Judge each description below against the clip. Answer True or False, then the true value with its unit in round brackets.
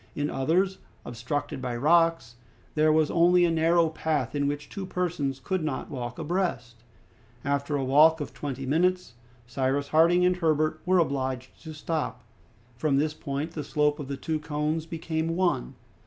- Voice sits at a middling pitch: True (155 Hz)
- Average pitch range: True (3.2 semitones)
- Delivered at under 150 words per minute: False (165 wpm)